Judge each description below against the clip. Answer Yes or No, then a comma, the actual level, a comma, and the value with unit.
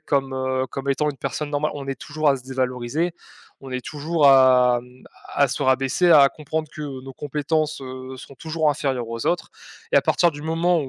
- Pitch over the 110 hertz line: Yes, medium, 140 Hz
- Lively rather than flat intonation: No, average, 2.7 semitones